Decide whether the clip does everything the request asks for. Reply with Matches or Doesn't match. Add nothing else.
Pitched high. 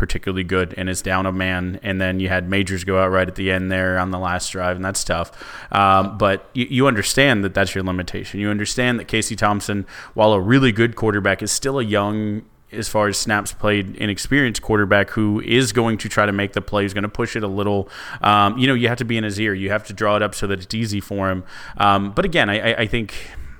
Doesn't match